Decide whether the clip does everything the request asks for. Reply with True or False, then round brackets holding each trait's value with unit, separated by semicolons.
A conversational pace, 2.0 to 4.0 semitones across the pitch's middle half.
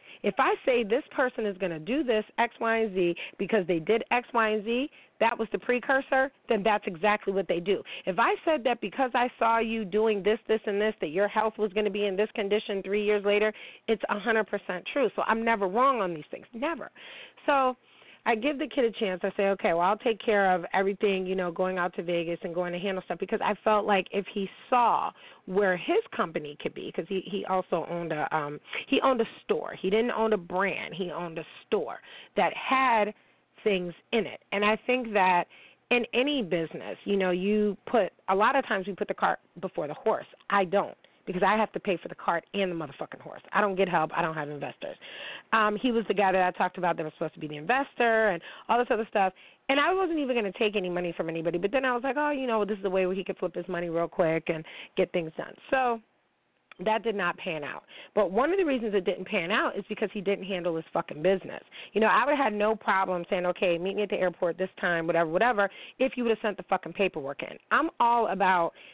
False (250 wpm; 3.7 semitones)